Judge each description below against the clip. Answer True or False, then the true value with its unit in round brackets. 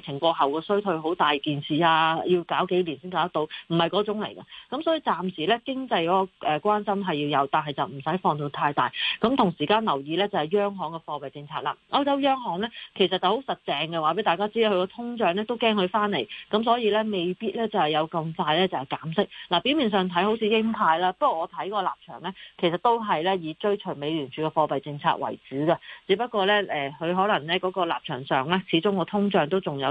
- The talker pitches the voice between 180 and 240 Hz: True (185 Hz)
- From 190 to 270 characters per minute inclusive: False (355 characters per minute)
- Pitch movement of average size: True (4.8 semitones)